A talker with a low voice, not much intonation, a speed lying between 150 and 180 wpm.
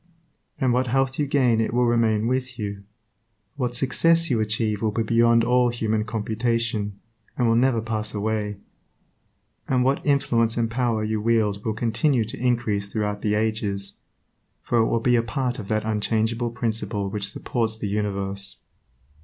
Yes: low, 115 Hz; narrow, 2.3 semitones; average, 165 wpm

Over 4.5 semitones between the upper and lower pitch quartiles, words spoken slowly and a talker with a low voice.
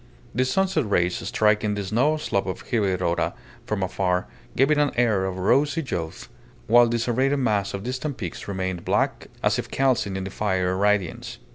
No: average, 5.2 semitones; average, 175 wpm; low, 105 Hz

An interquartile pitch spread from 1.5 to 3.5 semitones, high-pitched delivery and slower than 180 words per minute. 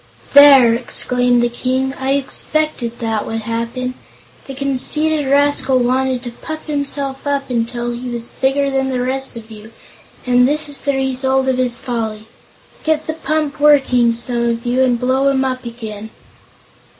Yes: narrow, 2.5 semitones; very high, 255 Hz; average, 160 wpm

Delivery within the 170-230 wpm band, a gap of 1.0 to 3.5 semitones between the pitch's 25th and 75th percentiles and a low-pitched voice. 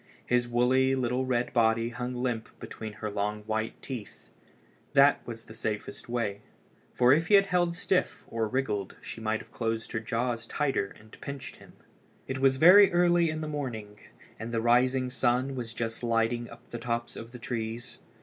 Yes: average, 180 wpm; average, 2.7 semitones; low, 120 Hz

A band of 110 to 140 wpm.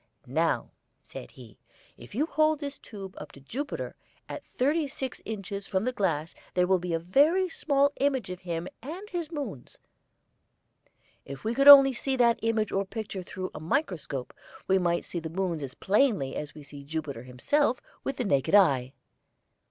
No: average, 175 wpm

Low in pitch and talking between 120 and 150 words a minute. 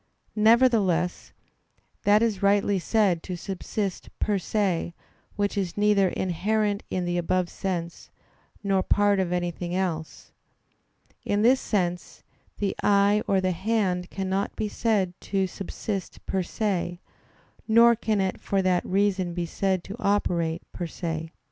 No: high, 190 Hz; slow, 135 wpm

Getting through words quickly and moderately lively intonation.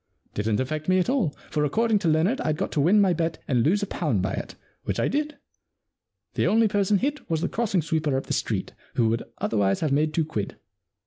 No: fast, 230 wpm; wide, 6.3 semitones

